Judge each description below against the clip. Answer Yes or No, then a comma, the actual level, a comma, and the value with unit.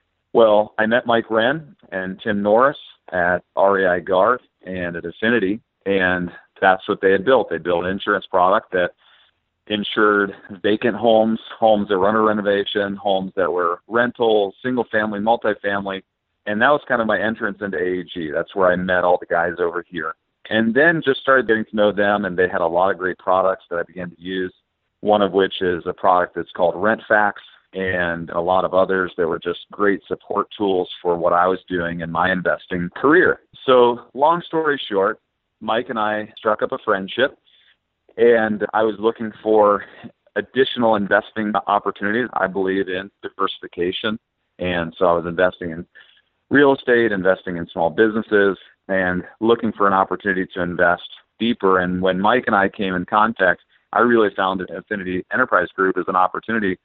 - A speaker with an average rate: Yes, average, 180 wpm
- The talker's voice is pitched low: Yes, low, 100 Hz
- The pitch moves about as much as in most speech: Yes, average, 3.0 semitones